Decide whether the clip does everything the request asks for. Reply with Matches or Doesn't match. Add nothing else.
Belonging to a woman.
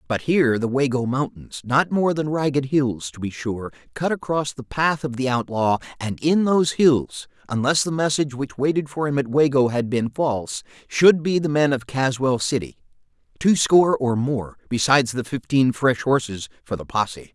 Doesn't match